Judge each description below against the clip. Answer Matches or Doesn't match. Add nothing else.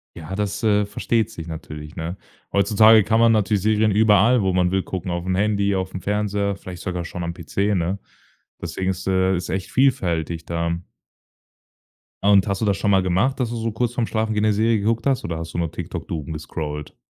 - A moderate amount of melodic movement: Matches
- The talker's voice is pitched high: Doesn't match